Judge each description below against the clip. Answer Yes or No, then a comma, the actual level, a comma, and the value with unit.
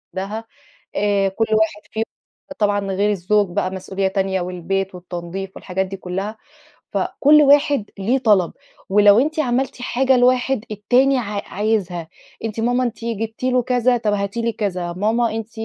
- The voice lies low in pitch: No, high, 210 Hz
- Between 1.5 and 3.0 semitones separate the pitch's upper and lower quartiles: No, average, 3.9 semitones